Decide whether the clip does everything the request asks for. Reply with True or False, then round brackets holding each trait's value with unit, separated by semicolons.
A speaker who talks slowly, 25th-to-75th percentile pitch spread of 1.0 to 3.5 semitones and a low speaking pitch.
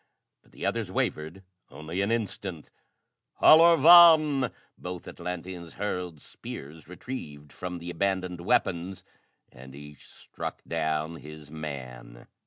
False (115 wpm; 4.1 semitones; 85 Hz)